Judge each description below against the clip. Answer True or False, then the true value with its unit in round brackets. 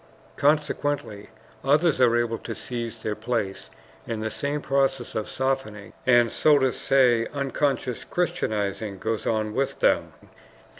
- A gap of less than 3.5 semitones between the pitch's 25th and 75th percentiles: False (3.9 semitones)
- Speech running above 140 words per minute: False (135 wpm)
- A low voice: True (120 Hz)